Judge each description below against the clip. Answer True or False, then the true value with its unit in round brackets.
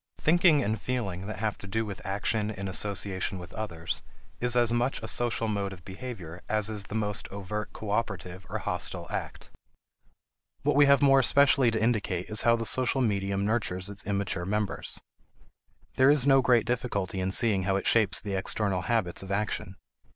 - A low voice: True (105 Hz)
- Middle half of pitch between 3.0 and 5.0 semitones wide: True (3.5 semitones)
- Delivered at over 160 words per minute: True (180 wpm)